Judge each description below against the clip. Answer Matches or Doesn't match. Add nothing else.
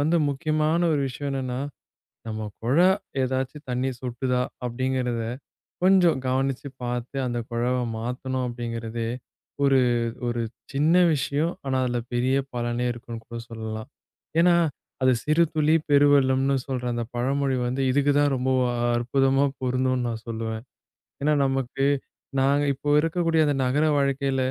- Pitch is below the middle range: Matches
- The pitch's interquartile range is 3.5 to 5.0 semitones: Doesn't match